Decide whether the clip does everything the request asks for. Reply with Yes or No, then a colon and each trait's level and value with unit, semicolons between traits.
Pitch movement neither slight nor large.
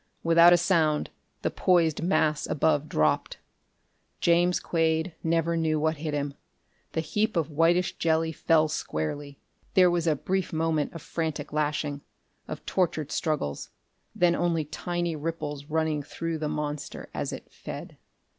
No: narrow, 2.0 semitones